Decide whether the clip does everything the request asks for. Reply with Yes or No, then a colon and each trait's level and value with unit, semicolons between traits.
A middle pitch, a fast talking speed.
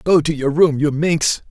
Yes: medium, 155 Hz; fast, 240 wpm